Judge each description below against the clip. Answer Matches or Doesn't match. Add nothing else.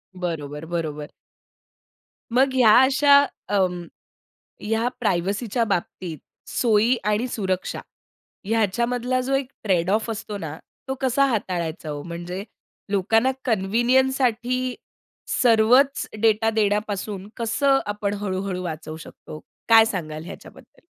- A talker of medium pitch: Doesn't match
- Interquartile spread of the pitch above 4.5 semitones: Matches